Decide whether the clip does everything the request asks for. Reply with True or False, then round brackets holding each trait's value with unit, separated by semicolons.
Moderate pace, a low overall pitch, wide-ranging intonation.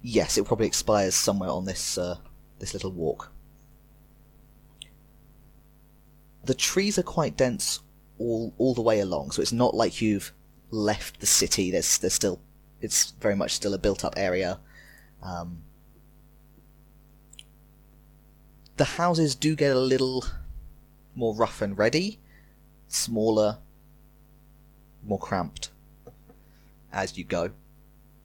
False (120 wpm; 90 Hz; 6.9 semitones)